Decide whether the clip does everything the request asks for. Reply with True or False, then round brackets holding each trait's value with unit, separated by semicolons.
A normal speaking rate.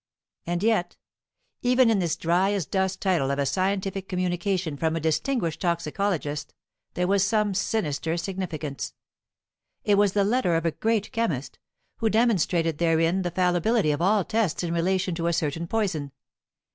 True (160 wpm)